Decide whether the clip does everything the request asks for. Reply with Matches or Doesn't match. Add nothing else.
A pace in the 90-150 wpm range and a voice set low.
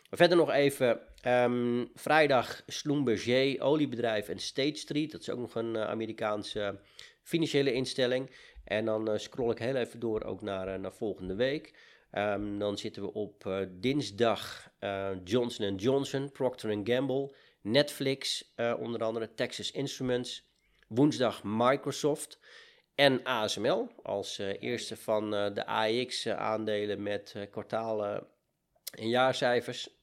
Matches